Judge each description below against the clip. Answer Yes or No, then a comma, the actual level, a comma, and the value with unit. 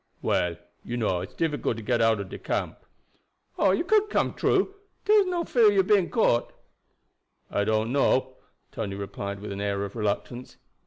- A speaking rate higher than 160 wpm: Yes, average, 180 wpm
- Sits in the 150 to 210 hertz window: No, low, 120 Hz